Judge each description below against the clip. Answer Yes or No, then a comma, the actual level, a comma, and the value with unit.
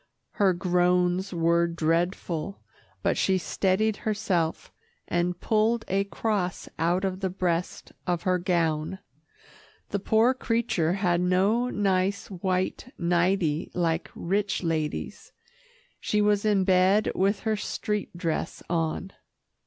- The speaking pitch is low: No, medium, 185 Hz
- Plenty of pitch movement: No, average, 2.7 semitones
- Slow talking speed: Yes, slow, 120 wpm